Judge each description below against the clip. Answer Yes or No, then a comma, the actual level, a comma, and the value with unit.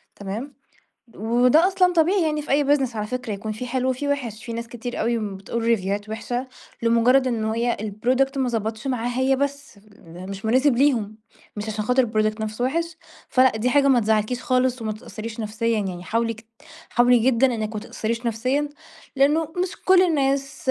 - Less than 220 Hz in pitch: No, high, 240 Hz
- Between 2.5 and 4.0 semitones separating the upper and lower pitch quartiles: Yes, average, 3.7 semitones